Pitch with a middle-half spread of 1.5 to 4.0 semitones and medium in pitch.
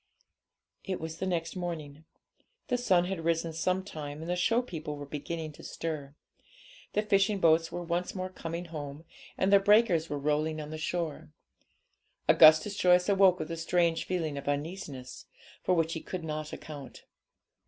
Yes: average, 3.0 semitones; medium, 165 Hz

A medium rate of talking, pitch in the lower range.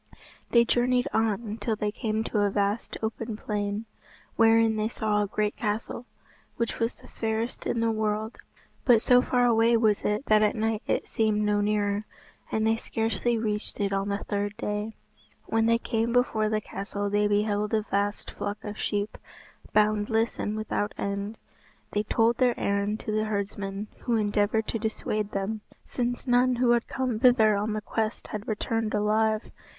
No: average, 175 wpm; high, 215 Hz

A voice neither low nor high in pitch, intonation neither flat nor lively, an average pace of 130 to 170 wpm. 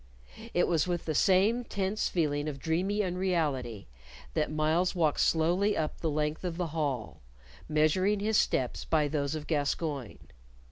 Yes: medium, 160 Hz; average, 3.4 semitones; average, 150 wpm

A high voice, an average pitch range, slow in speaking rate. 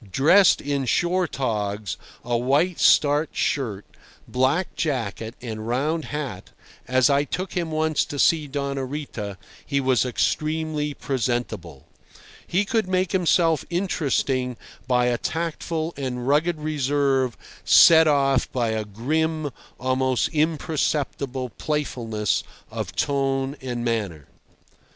No: medium, 140 Hz; average, 4.3 semitones; slow, 120 wpm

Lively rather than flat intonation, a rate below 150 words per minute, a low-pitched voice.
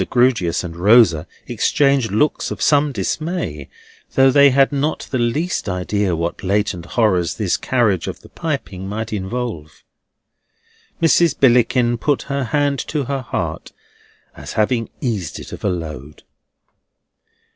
Yes: wide, 6.9 semitones; slow, 135 wpm; low, 115 Hz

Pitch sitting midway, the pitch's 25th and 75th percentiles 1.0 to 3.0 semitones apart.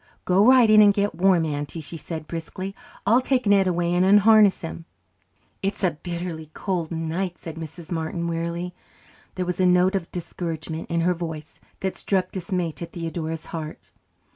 Yes: medium, 175 Hz; narrow, 2.6 semitones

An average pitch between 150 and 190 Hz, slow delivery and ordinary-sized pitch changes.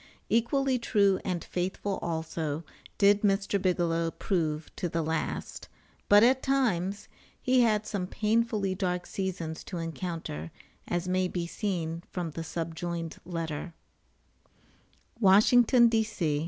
Yes: medium, 185 Hz; slow, 120 wpm; average, 4.1 semitones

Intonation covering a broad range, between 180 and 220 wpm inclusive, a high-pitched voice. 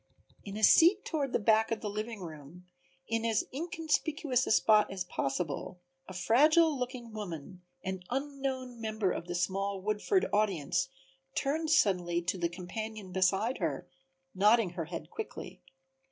No: wide, 5.8 semitones; average, 150 wpm; high, 215 Hz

